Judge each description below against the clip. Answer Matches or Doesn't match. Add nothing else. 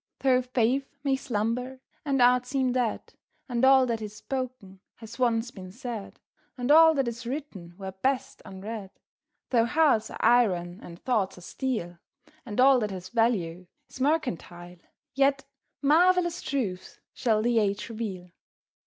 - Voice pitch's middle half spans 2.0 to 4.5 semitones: Doesn't match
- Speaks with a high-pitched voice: Matches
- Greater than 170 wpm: Doesn't match